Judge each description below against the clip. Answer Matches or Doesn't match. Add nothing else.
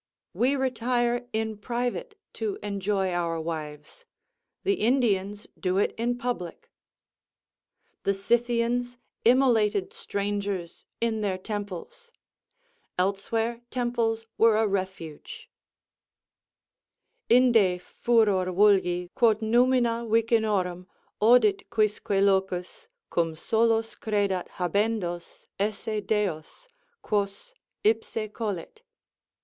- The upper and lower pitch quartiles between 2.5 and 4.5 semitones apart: Matches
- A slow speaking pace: Matches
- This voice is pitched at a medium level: Doesn't match